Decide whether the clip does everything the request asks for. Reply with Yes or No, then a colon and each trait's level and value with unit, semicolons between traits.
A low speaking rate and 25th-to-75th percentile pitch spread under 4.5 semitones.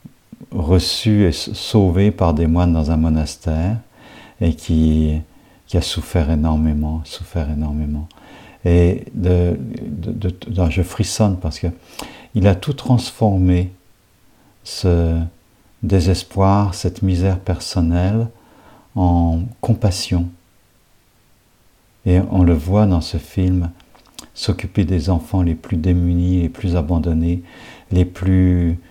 Yes: slow, 110 wpm; average, 2.7 semitones